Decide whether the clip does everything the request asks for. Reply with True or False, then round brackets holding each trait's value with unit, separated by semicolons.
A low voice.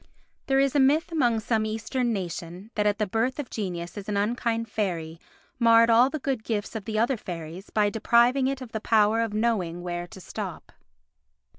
False (220 Hz)